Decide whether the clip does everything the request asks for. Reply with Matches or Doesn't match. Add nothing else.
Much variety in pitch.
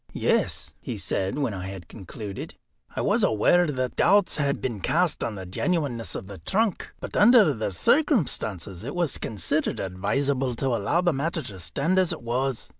Matches